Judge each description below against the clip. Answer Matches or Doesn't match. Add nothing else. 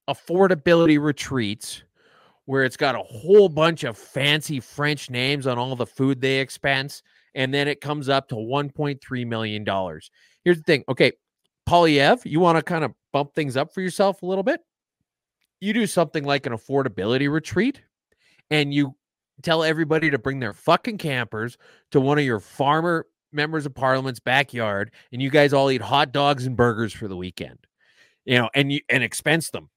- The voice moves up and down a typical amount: Matches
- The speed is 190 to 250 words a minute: Doesn't match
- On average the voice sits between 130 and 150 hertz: Matches